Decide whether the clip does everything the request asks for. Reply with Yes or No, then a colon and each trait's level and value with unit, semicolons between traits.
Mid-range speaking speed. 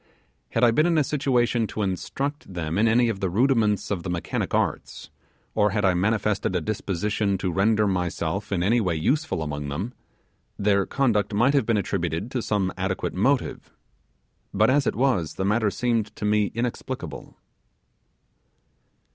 Yes: average, 165 wpm